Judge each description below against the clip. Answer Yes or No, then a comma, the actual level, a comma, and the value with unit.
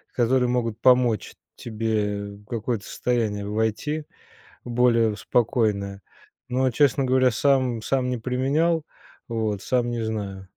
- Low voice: Yes, low, 120 Hz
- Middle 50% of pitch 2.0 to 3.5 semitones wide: Yes, average, 2.9 semitones